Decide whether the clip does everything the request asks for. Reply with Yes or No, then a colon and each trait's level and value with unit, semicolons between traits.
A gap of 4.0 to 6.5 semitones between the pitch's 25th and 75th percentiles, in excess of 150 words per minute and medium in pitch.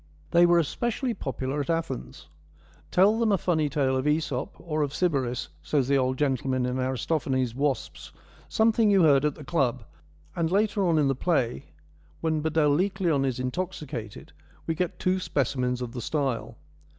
Yes: average, 4.9 semitones; average, 180 wpm; medium, 150 Hz